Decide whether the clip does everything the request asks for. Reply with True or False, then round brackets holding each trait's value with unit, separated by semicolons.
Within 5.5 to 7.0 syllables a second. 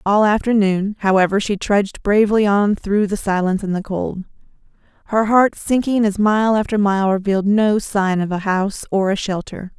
False (5.1 syllables/s)